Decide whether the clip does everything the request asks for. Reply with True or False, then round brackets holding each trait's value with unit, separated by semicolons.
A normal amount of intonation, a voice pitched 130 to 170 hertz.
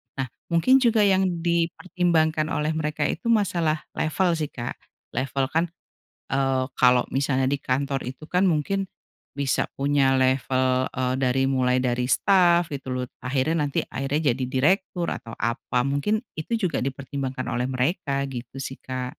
True (4.4 semitones; 140 Hz)